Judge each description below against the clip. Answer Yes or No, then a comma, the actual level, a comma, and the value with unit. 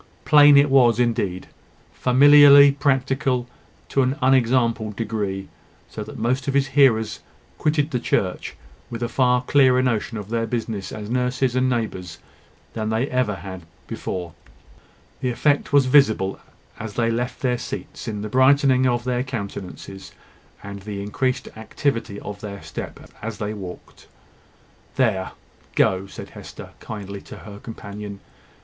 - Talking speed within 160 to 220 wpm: No, average, 145 wpm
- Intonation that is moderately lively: Yes, average, 4.0 semitones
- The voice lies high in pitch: No, low, 120 Hz